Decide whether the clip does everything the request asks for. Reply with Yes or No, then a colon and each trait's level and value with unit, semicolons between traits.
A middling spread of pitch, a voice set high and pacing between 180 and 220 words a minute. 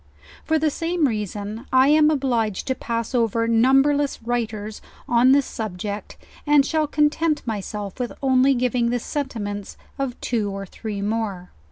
No: average, 4.5 semitones; high, 240 Hz; average, 150 wpm